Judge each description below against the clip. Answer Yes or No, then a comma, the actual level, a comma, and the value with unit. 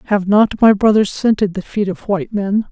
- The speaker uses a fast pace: Yes, fast, 220 wpm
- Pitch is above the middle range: Yes, high, 205 Hz